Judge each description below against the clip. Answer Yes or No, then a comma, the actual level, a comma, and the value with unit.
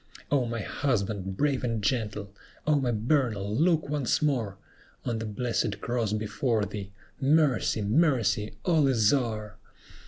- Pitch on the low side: Yes, low, 115 Hz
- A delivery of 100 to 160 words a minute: Yes, slow, 135 wpm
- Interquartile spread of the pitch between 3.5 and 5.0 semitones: Yes, average, 4.7 semitones